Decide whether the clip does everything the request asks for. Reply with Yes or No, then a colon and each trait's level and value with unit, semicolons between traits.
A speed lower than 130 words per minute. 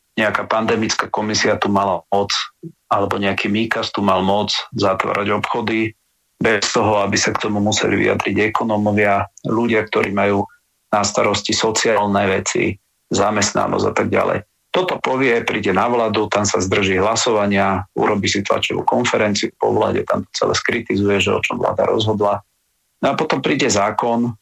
No: average, 155 wpm